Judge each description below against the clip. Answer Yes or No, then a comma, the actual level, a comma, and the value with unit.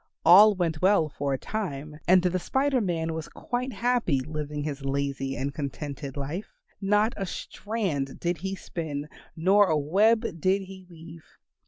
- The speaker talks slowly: No, average, 160 wpm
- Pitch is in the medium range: Yes, medium, 170 Hz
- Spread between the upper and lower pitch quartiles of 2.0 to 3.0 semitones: No, wide, 5.4 semitones